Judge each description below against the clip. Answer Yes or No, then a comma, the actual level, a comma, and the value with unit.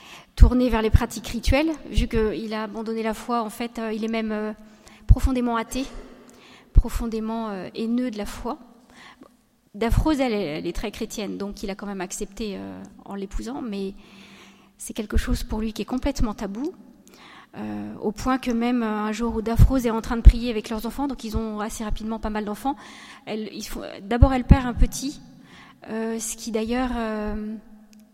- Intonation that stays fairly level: Yes, narrow, 2.0 semitones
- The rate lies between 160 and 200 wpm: Yes, average, 190 wpm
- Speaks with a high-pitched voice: Yes, high, 225 Hz